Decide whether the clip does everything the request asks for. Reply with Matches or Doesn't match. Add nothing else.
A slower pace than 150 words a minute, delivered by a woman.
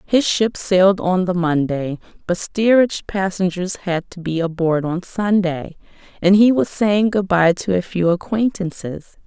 Doesn't match